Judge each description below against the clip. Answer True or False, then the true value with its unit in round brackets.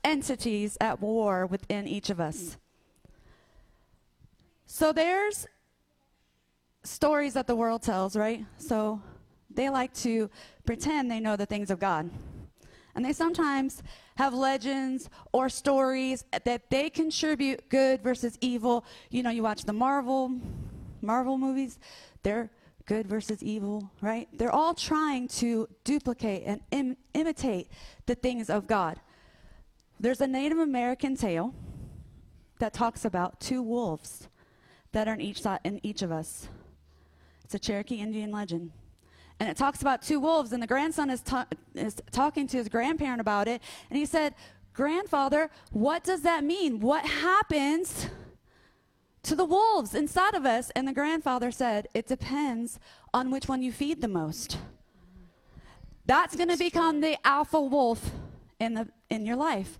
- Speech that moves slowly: False (145 wpm)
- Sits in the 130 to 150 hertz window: False (250 Hz)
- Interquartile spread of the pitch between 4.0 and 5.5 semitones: True (5.1 semitones)